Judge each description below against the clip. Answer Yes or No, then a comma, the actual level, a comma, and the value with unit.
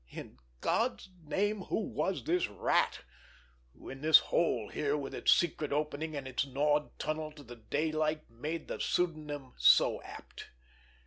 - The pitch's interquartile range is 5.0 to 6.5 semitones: No, narrow, 2.5 semitones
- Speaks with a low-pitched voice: No, medium, 150 Hz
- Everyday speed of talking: Yes, average, 150 wpm